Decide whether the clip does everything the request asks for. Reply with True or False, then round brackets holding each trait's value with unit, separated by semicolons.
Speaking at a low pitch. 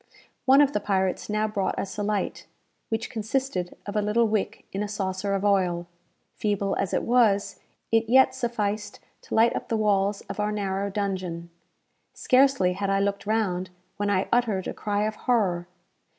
False (205 Hz)